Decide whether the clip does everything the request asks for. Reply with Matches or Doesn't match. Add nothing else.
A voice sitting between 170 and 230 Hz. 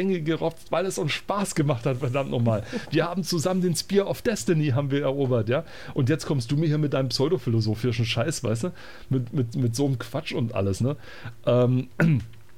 Doesn't match